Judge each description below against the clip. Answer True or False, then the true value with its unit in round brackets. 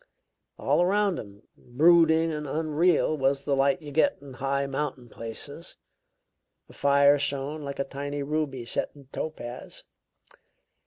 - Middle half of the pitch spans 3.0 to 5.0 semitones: False (2.5 semitones)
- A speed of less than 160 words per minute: True (140 wpm)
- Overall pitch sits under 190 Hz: True (140 Hz)